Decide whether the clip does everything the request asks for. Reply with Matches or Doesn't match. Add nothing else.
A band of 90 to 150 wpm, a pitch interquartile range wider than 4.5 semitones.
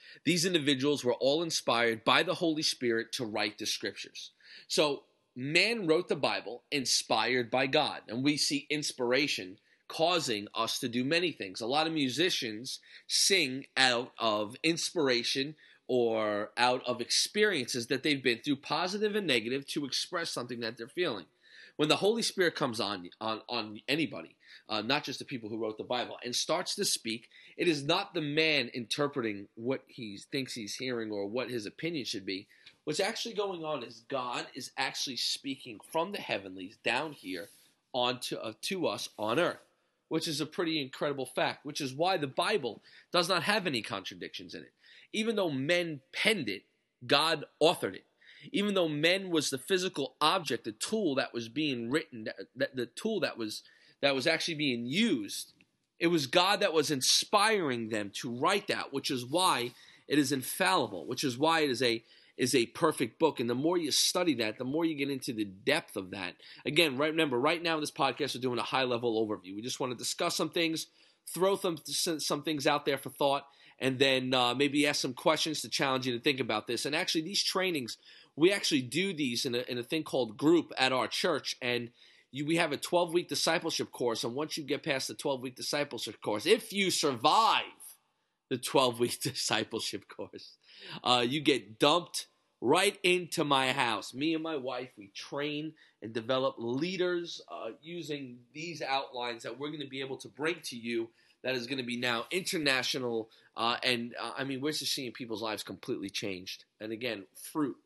Doesn't match